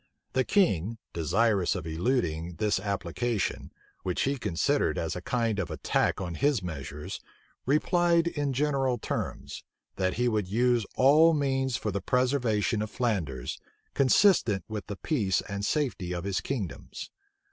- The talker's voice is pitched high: No, low, 110 Hz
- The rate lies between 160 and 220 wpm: No, average, 145 wpm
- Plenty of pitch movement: Yes, wide, 6.3 semitones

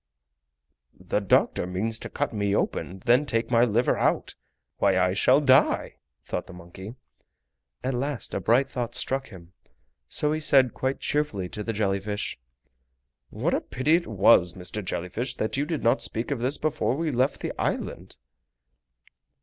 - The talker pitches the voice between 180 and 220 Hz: No, low, 115 Hz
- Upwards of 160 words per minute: Yes, average, 175 wpm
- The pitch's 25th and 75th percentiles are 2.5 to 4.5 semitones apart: No, wide, 5.5 semitones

